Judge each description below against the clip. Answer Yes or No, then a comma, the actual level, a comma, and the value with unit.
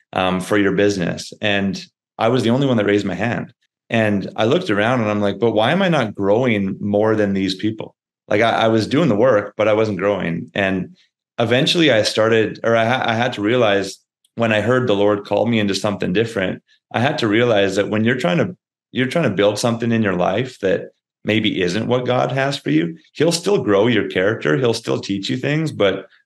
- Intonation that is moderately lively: Yes, average, 3.6 semitones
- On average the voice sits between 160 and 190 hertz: No, low, 110 Hz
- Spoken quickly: Yes, fast, 225 wpm